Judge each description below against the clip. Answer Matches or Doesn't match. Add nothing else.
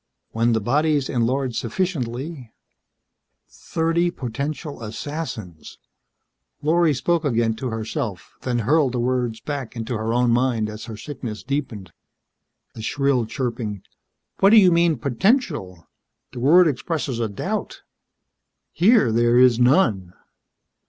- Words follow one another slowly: Matches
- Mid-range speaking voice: Doesn't match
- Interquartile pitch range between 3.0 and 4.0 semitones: Doesn't match